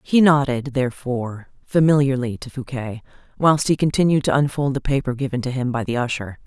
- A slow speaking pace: No, average, 175 wpm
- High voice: No, low, 135 Hz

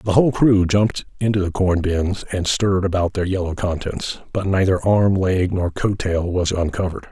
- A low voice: Yes, very low, 95 Hz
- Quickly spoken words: No, average, 195 wpm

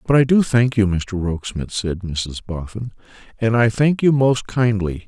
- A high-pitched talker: No, low, 110 Hz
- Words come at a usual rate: Yes, average, 190 wpm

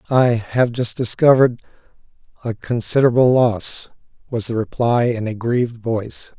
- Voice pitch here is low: Yes, low, 120 Hz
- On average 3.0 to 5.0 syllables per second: Yes, 4.9 syllables/s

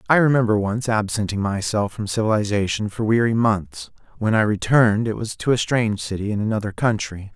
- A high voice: No, low, 110 Hz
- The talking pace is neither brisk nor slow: Yes, average, 180 wpm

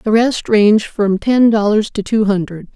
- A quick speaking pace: No, average, 195 wpm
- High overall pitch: Yes, high, 215 Hz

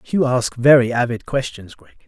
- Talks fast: No, average, 175 wpm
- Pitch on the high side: No, low, 125 Hz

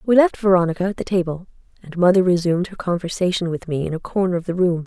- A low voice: No, medium, 180 Hz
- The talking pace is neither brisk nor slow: No, fast, 235 wpm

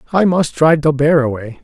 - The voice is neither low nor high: Yes, medium, 150 Hz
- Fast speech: Yes, fast, 220 wpm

